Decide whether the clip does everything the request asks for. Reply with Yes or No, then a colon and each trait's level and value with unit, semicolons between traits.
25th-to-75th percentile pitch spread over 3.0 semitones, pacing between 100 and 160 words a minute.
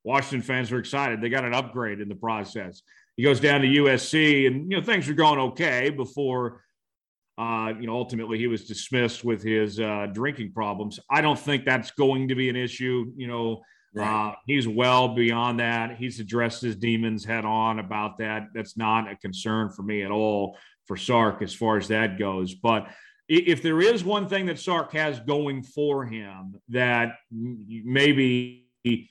No: average, 3.4 semitones; average, 185 wpm